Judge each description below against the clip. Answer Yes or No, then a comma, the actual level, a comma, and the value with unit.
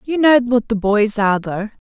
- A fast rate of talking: Yes, fast, 225 wpm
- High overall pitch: Yes, high, 225 Hz